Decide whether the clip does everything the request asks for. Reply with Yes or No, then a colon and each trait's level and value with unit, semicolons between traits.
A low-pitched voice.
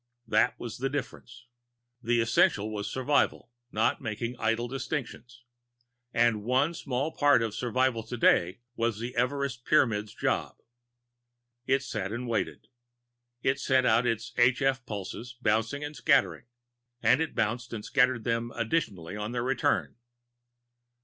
Yes: low, 120 Hz